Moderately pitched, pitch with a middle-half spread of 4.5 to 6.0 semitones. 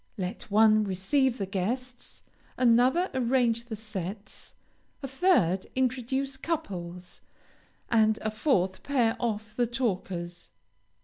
No: high, 225 Hz; average, 4.8 semitones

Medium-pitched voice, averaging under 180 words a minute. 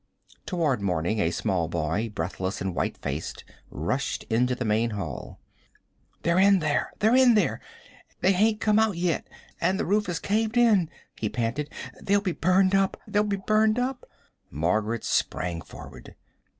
Yes: medium, 170 Hz; average, 160 wpm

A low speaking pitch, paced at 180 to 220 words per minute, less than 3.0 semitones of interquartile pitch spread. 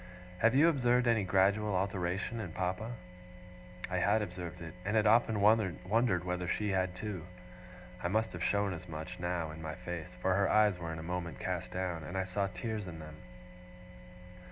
No: very low, 95 Hz; average, 185 wpm; average, 3.3 semitones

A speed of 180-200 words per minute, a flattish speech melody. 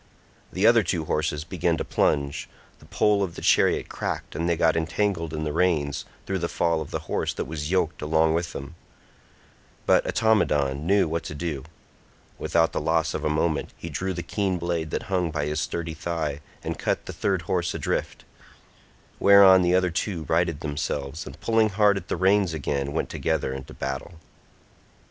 No: average, 185 wpm; average, 3.3 semitones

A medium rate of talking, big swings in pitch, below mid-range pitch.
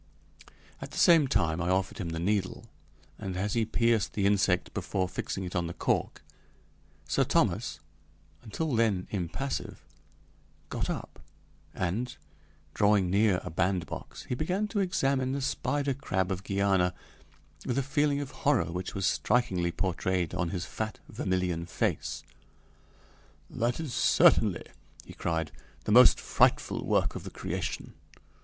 Yes: average, 145 wpm; wide, 6.0 semitones; low, 100 Hz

